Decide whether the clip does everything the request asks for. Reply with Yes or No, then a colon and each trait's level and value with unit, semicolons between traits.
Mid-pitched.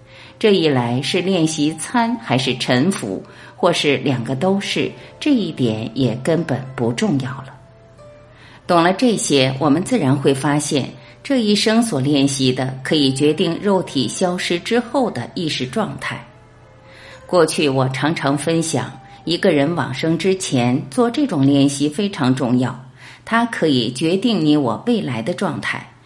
Yes: medium, 145 Hz